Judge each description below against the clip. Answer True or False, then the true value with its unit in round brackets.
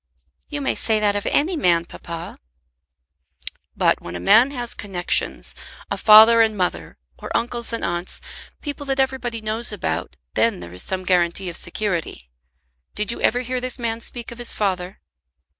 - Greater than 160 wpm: True (170 wpm)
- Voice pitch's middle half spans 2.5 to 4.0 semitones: False (5.1 semitones)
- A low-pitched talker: False (215 Hz)